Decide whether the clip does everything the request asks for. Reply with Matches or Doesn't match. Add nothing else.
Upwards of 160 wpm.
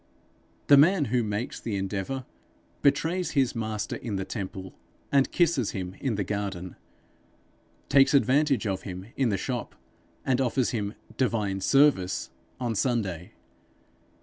Doesn't match